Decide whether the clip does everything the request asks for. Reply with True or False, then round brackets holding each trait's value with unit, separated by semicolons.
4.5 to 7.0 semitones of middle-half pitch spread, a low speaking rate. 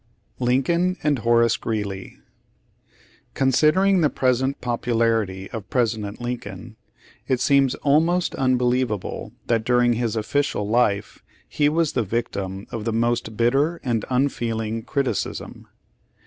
False (3.5 semitones; 120 wpm)